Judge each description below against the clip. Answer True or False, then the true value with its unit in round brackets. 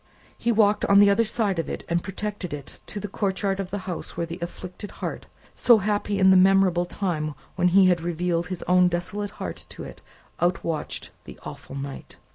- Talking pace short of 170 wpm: False (200 wpm)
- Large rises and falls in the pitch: False (2.8 semitones)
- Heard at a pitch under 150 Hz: False (185 Hz)